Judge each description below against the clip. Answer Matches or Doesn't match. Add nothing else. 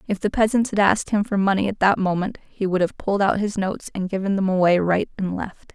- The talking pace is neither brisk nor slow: Doesn't match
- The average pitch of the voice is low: Doesn't match